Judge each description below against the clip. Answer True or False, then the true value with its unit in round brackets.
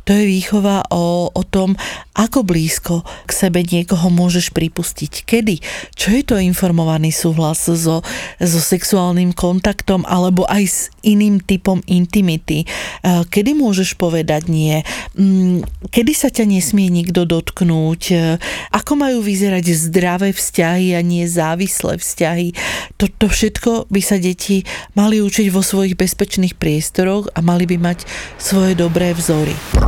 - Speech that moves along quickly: False (130 wpm)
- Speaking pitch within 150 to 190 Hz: True (185 Hz)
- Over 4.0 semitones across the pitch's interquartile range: False (2.7 semitones)